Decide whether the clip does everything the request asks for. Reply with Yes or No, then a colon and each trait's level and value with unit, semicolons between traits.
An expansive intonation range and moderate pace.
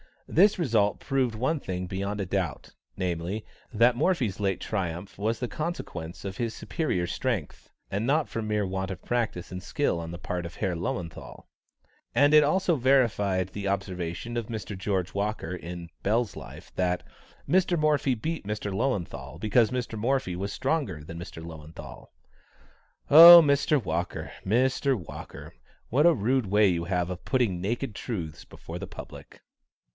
Yes: wide, 6.1 semitones; average, 160 wpm